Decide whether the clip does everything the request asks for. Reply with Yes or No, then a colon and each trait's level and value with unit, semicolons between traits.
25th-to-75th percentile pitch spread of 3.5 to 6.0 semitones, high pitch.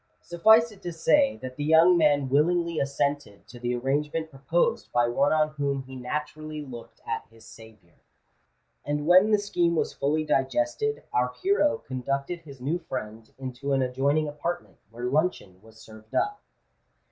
No: average, 4.6 semitones; medium, 145 Hz